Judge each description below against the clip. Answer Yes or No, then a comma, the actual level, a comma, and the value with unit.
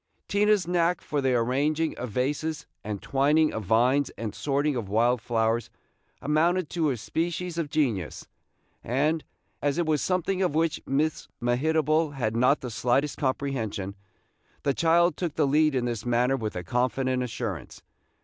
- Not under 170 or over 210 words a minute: No, average, 160 wpm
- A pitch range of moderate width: Yes, average, 4.6 semitones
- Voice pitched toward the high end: No, medium, 140 Hz